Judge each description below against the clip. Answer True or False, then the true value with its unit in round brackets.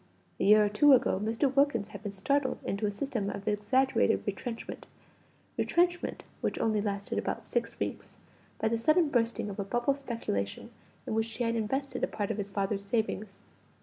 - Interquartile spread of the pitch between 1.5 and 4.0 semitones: False (4.4 semitones)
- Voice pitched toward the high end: True (220 Hz)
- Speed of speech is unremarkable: True (180 wpm)